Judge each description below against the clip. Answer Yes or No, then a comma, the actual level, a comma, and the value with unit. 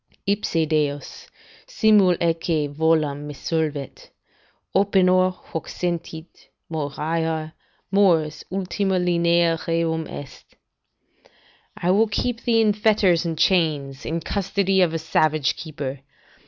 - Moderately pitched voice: Yes, medium, 165 Hz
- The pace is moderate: No, slow, 110 wpm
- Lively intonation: No, average, 3.4 semitones